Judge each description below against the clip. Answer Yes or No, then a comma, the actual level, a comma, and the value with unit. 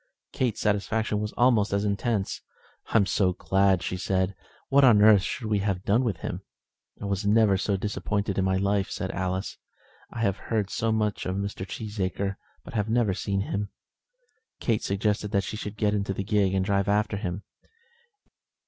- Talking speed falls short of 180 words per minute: No, average, 185 wpm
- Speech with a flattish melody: Yes, narrow, 1.8 semitones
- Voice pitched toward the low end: Yes, low, 100 Hz